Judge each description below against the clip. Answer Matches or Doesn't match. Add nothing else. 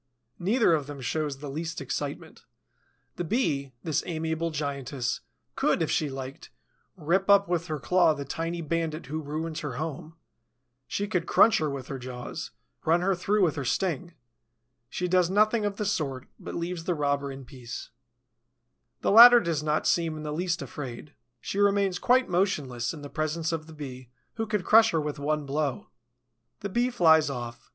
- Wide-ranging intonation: Doesn't match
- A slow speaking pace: Doesn't match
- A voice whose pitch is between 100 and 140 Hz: Doesn't match